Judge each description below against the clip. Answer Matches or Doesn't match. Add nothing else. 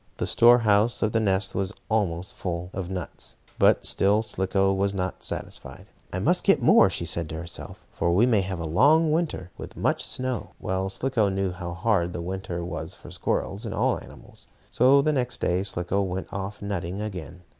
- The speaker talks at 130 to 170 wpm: Doesn't match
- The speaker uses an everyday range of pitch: Matches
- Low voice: Matches